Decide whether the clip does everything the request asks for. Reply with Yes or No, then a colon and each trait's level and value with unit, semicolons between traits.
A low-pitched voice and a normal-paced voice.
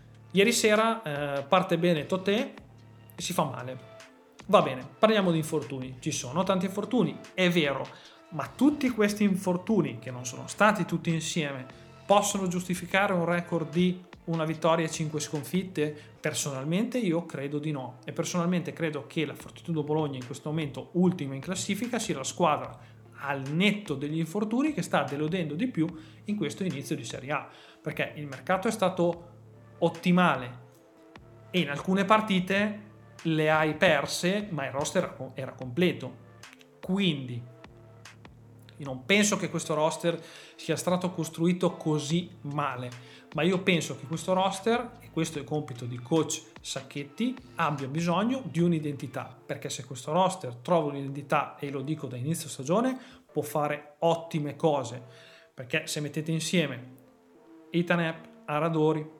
No: medium, 160 Hz; average, 150 wpm